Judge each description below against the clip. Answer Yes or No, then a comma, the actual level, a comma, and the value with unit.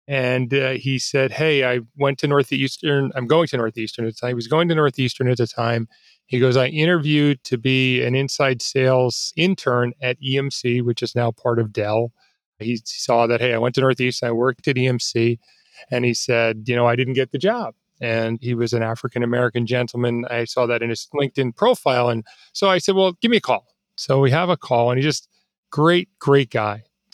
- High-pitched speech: No, low, 125 Hz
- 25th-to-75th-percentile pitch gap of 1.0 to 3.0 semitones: Yes, narrow, 2.6 semitones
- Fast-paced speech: Yes, fast, 210 wpm